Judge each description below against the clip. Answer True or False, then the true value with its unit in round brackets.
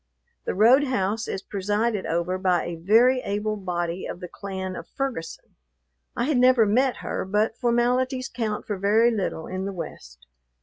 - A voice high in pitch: True (210 Hz)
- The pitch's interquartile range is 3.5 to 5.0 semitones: True (4.4 semitones)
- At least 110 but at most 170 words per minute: True (165 wpm)